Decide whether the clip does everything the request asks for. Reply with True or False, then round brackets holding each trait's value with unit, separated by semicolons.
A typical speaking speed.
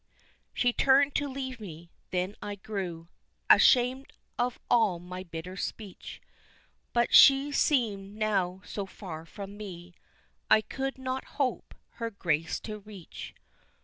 False (130 wpm)